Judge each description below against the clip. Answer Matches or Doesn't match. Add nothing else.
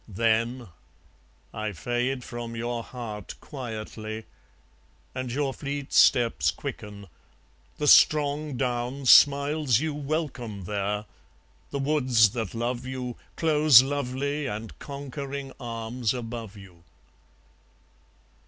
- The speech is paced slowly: Matches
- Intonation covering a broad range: Doesn't match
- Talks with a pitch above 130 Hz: Doesn't match